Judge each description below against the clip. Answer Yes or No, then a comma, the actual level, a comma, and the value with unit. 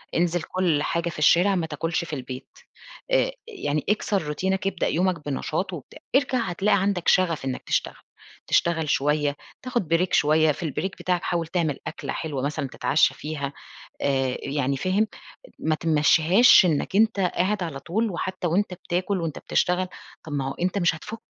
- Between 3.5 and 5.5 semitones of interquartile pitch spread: Yes, average, 3.9 semitones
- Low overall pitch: No, medium, 170 Hz